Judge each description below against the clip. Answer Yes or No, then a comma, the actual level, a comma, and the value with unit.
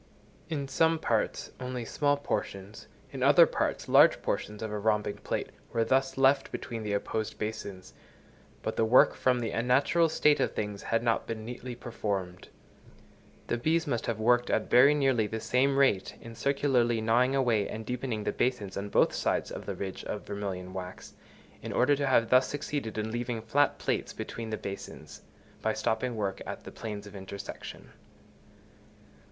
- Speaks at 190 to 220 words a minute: No, average, 175 wpm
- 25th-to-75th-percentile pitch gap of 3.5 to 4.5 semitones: Yes, average, 3.8 semitones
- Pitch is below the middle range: Yes, low, 115 Hz